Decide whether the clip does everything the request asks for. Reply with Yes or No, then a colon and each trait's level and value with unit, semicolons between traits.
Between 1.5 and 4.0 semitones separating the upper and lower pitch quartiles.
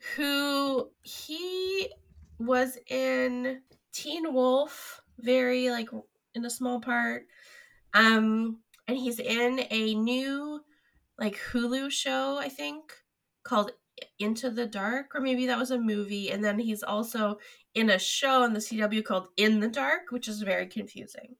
Yes: average, 3.7 semitones